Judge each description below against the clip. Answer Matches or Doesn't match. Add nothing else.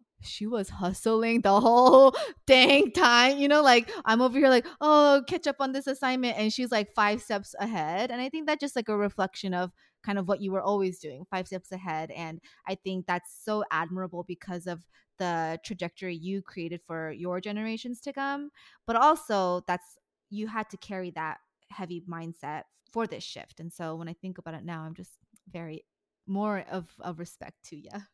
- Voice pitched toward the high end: Matches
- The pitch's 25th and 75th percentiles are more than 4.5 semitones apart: Matches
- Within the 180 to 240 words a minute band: Matches